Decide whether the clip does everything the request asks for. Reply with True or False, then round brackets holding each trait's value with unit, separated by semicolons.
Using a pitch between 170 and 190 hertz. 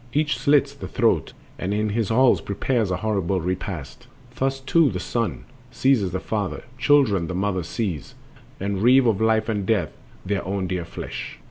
False (105 Hz)